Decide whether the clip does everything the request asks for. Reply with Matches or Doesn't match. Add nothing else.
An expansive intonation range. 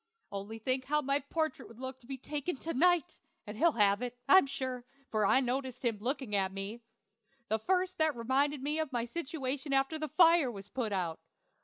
Doesn't match